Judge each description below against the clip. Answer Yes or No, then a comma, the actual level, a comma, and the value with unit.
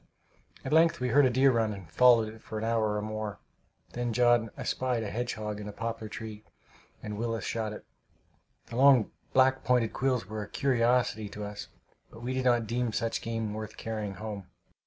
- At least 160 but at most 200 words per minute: Yes, average, 195 wpm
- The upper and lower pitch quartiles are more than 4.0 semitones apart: No, narrow, 2.5 semitones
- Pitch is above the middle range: No, low, 115 Hz